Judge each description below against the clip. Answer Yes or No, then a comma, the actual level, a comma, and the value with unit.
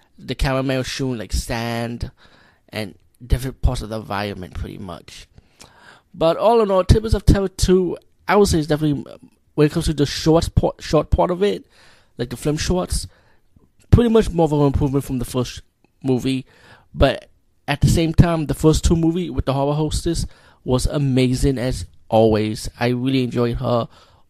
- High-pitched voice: No, low, 130 Hz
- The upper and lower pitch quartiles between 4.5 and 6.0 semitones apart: Yes, average, 5.0 semitones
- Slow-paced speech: No, average, 180 wpm